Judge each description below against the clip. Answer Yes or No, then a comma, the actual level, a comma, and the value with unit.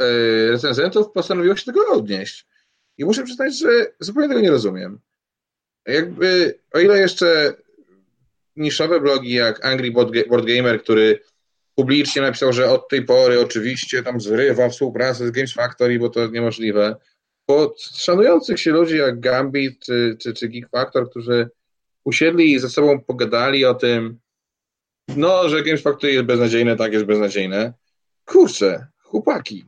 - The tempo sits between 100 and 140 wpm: No, average, 150 wpm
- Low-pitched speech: Yes, low, 130 Hz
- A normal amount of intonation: No, wide, 6.0 semitones